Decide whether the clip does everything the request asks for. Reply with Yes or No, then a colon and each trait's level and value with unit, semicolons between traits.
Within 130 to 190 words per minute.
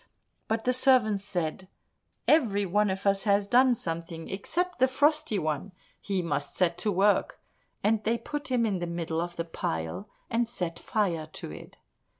Yes: average, 170 wpm